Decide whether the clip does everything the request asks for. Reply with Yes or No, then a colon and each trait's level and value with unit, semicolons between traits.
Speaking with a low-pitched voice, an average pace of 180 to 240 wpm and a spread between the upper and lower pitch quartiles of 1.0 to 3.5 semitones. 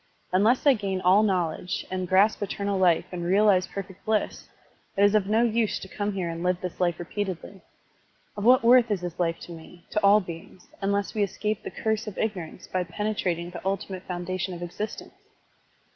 No: high, 190 Hz; average, 190 wpm; average, 2.8 semitones